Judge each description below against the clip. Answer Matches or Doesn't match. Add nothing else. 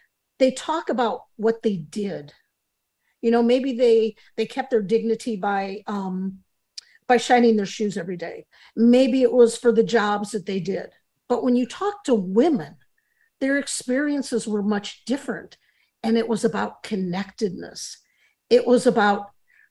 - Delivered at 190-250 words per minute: Doesn't match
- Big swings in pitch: Doesn't match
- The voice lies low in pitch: Doesn't match